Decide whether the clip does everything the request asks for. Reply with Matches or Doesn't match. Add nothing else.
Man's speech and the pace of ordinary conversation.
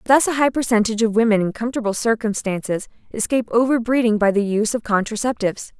Doesn't match